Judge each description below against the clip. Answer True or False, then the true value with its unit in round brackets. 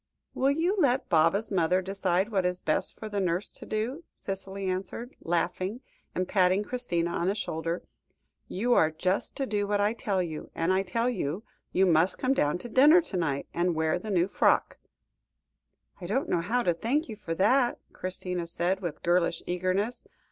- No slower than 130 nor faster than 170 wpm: False (185 wpm)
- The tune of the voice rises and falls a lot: False (4.1 semitones)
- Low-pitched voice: False (190 Hz)